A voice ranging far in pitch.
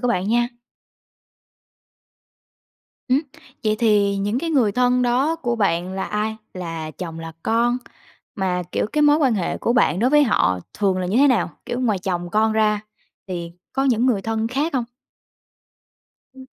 No: average, 4.7 semitones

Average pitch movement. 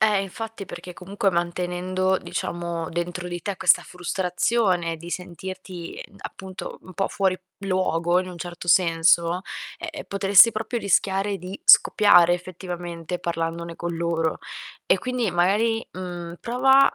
No: narrow, 2.3 semitones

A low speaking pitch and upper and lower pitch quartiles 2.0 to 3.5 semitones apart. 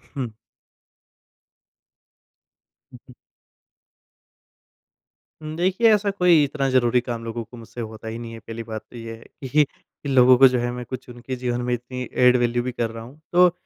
Yes: low, 125 Hz; average, 2.7 semitones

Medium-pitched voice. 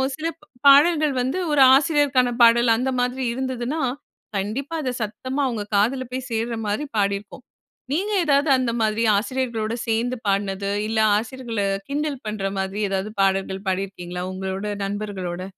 No: high, 230 Hz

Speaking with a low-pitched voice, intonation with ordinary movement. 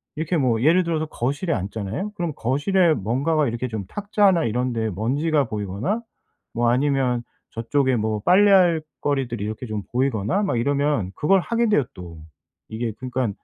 No: low, 130 Hz; wide, 6.5 semitones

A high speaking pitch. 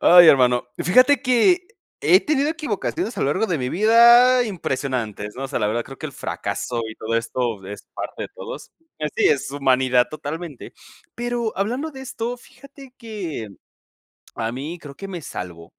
No: medium, 170 Hz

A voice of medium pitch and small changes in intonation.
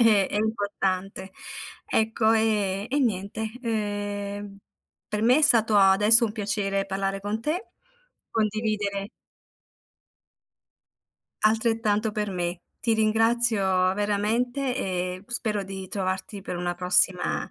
No: high, 205 Hz; narrow, 2.3 semitones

